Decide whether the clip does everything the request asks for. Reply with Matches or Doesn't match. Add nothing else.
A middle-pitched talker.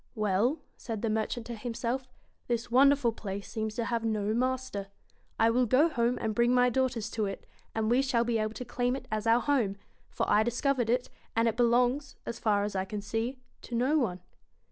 Doesn't match